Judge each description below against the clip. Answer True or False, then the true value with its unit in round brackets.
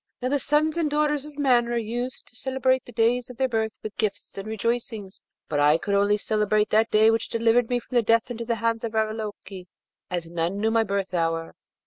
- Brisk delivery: True (215 wpm)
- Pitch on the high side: True (225 Hz)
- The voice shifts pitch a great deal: False (3.0 semitones)